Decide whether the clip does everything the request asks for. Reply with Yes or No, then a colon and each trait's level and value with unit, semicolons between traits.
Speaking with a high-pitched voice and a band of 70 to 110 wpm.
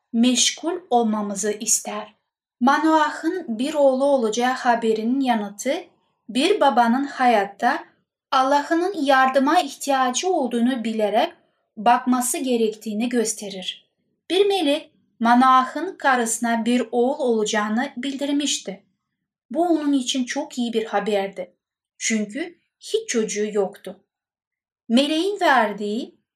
Yes: very high, 250 Hz; slow, 95 wpm